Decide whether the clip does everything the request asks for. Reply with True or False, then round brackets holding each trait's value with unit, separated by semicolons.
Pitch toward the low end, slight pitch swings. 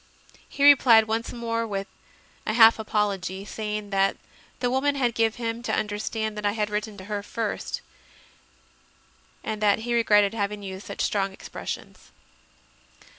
False (215 Hz; 2.0 semitones)